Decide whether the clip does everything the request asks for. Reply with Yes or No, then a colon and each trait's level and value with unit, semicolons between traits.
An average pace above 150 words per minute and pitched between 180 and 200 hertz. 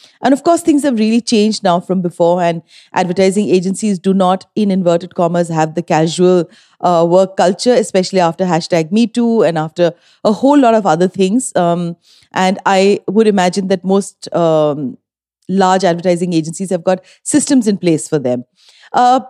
Yes: average, 170 wpm; medium, 185 Hz